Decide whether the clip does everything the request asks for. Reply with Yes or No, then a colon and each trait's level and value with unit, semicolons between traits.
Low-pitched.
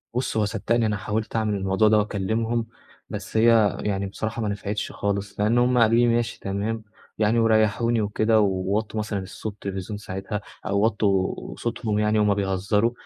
Yes: low, 105 Hz